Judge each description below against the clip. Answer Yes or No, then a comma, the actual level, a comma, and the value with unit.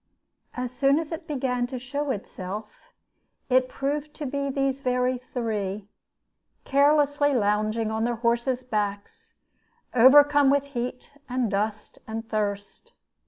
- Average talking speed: No, slow, 125 wpm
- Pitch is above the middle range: Yes, very high, 250 Hz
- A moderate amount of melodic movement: Yes, average, 4.2 semitones